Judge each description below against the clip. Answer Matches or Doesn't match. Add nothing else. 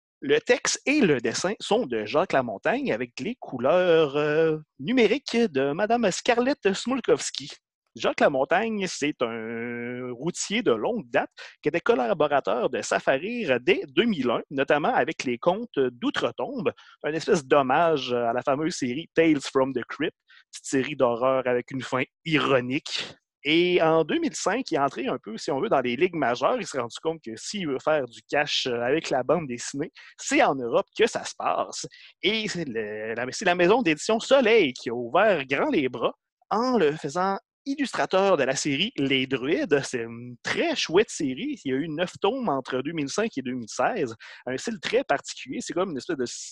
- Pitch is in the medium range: Matches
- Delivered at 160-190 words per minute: Matches